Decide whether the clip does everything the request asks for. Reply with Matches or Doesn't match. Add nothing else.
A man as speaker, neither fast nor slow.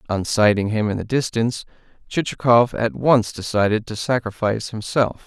Matches